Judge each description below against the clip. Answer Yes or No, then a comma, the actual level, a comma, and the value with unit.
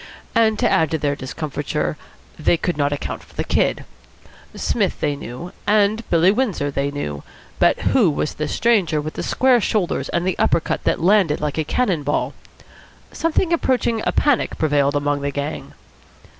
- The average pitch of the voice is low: No, medium, 160 Hz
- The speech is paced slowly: No, average, 175 wpm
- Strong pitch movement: Yes, wide, 6.7 semitones